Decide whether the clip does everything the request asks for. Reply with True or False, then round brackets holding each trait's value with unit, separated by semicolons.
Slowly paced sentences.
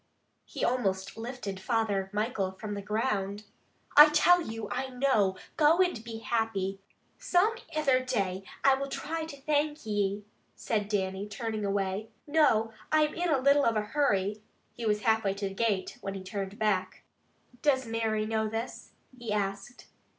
False (165 wpm)